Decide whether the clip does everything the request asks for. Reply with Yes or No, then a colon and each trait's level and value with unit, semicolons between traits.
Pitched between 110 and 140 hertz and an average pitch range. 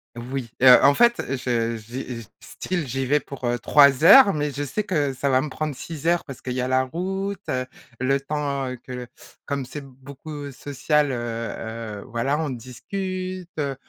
Yes: low, 135 Hz; average, 3.2 semitones